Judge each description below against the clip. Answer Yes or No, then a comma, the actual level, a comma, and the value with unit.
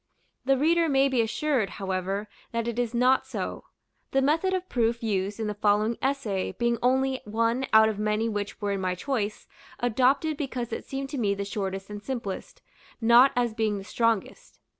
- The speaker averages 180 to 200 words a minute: Yes, average, 185 wpm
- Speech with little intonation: No, average, 4.2 semitones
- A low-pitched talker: No, high, 230 Hz